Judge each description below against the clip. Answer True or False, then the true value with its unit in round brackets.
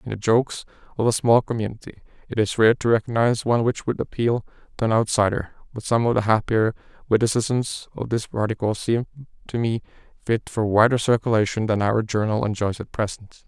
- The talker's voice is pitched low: True (110 Hz)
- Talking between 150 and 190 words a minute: True (185 wpm)